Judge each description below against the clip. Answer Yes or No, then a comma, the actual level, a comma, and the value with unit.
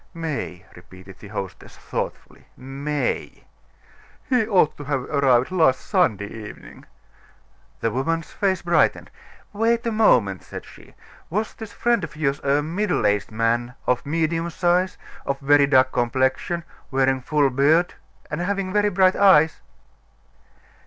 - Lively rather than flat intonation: Yes, wide, 5.9 semitones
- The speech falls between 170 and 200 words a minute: No, average, 140 wpm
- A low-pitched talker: No, medium, 150 Hz